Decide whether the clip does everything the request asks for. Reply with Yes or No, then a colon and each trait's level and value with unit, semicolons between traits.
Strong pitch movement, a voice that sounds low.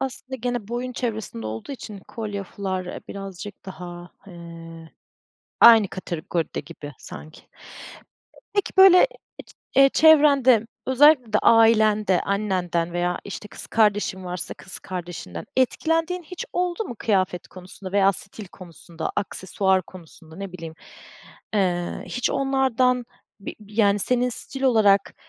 No: wide, 5.7 semitones; high, 200 Hz